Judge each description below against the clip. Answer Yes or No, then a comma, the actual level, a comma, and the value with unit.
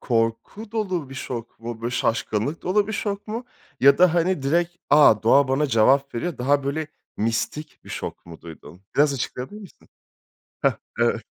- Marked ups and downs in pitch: Yes, wide, 7.1 semitones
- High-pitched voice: No, medium, 140 Hz